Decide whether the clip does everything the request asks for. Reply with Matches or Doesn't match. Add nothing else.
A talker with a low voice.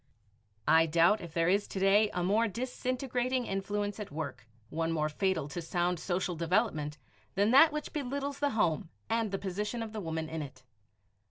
Doesn't match